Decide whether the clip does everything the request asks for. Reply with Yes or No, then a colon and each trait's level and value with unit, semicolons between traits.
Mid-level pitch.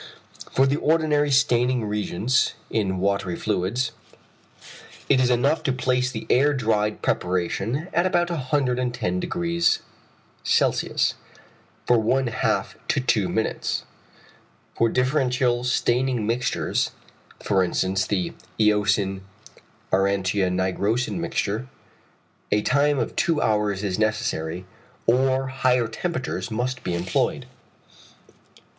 No: low, 120 Hz